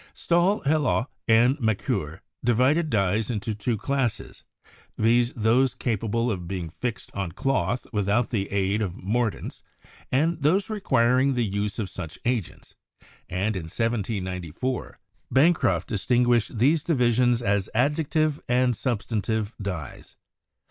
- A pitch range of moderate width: Yes, average, 4.3 semitones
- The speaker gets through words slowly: Yes, slow, 120 wpm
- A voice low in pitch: Yes, low, 115 Hz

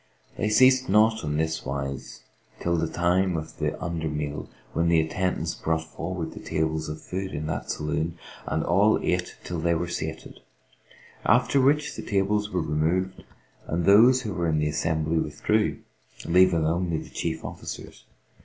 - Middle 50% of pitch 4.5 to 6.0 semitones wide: No, average, 3.4 semitones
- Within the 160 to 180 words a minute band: Yes, average, 165 wpm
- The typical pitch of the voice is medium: No, very low, 85 Hz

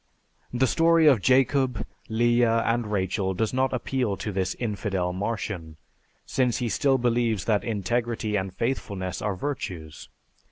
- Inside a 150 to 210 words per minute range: No, slow, 135 wpm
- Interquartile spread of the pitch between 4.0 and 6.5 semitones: Yes, average, 4.4 semitones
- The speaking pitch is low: Yes, low, 115 Hz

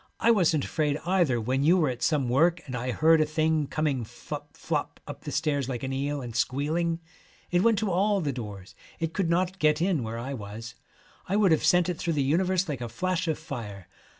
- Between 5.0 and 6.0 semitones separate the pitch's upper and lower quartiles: Yes, average, 5.3 semitones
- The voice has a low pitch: No, medium, 155 Hz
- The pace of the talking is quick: Yes, fast, 225 wpm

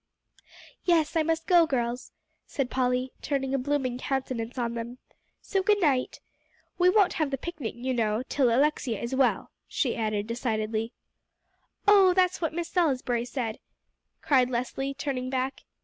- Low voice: No, very high, 260 Hz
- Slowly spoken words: No, average, 150 wpm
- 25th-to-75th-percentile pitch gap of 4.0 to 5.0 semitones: Yes, average, 4.5 semitones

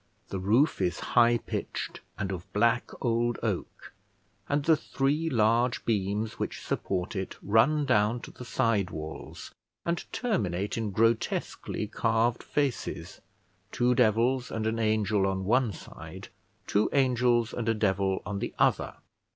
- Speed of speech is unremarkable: Yes, average, 145 wpm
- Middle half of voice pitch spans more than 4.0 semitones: No, average, 3.4 semitones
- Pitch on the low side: Yes, low, 115 Hz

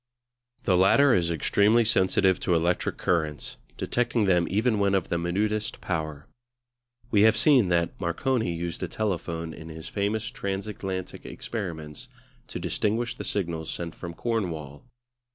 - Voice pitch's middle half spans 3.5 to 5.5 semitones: Yes, average, 4.3 semitones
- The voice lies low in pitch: Yes, very low, 95 Hz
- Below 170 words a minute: Yes, average, 140 wpm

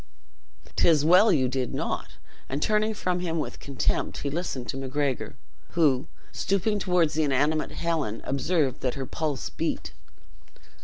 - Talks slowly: No, average, 145 wpm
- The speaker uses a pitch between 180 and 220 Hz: No, medium, 150 Hz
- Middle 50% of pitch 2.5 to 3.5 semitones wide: No, average, 4.6 semitones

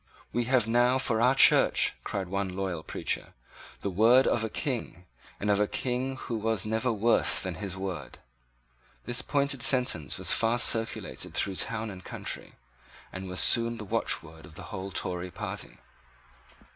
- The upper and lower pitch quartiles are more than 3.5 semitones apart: Yes, average, 4.4 semitones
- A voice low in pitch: Yes, low, 110 Hz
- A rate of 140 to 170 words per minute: Yes, average, 165 wpm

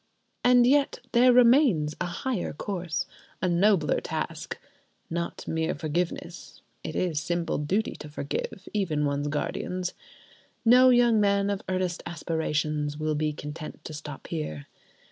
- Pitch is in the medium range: Yes, medium, 170 Hz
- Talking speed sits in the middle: No, slow, 130 wpm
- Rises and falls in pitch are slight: No, average, 5.2 semitones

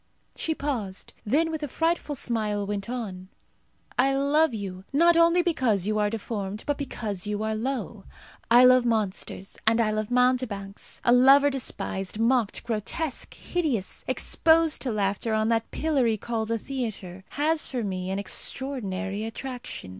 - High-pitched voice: Yes, high, 230 Hz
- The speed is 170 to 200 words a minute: No, average, 155 wpm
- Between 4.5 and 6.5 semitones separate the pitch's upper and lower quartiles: Yes, average, 4.9 semitones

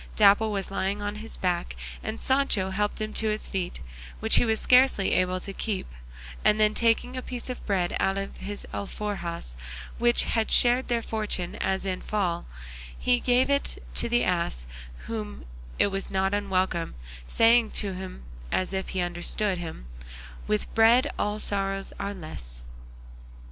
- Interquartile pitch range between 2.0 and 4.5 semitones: Yes, average, 3.2 semitones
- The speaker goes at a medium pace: Yes, average, 165 wpm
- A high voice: Yes, high, 200 Hz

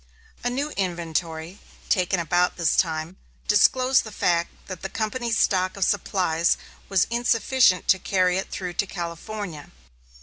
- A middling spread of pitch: Yes, average, 3.9 semitones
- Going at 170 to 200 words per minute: No, average, 140 wpm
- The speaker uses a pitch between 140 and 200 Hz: Yes, medium, 185 Hz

